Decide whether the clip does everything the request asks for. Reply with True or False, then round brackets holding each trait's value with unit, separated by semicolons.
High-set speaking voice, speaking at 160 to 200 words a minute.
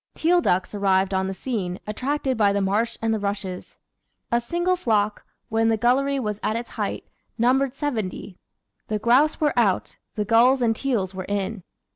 True (225 Hz; 175 wpm)